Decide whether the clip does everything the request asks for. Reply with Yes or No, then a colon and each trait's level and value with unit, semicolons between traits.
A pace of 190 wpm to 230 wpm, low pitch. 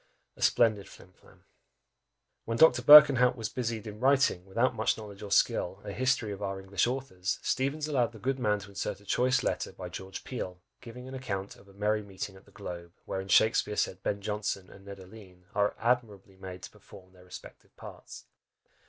Yes: average, 195 wpm; low, 105 Hz